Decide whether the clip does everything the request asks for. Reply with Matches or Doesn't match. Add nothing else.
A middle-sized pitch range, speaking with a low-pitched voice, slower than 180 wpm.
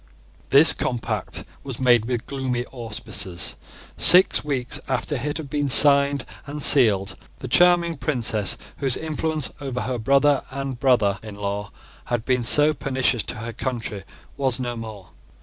Matches